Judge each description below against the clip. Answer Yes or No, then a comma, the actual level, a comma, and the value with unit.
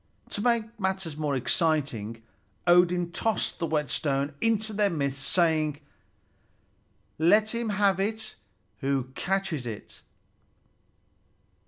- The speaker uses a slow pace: Yes, slow, 105 wpm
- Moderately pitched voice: Yes, medium, 170 Hz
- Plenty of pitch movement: Yes, wide, 6.3 semitones